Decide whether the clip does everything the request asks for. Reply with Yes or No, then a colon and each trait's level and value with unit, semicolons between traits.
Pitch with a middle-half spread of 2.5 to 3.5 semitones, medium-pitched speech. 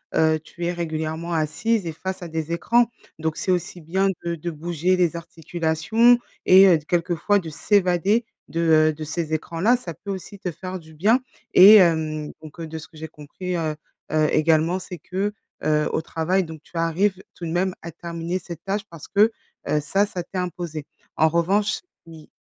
Yes: average, 2.8 semitones; medium, 170 Hz